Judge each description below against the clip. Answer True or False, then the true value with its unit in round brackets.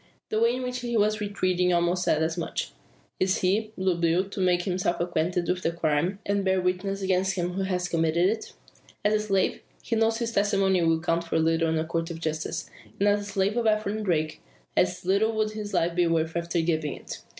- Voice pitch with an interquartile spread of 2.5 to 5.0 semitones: True (3.3 semitones)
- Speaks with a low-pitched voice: False (185 Hz)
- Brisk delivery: True (220 wpm)